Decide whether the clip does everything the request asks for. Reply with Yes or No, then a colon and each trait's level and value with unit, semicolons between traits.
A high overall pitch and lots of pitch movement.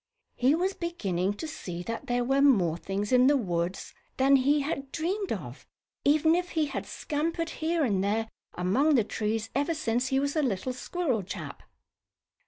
Yes: very high, 265 Hz; wide, 6.8 semitones